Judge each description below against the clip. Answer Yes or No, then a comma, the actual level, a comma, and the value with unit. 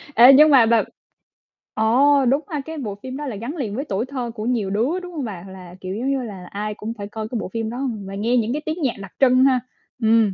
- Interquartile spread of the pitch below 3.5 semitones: No, average, 4.4 semitones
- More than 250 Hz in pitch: No, high, 235 Hz